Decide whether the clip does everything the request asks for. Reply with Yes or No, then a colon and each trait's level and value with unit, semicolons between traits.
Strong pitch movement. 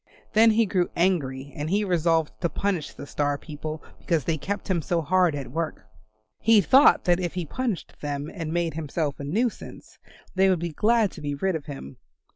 No: average, 4.4 semitones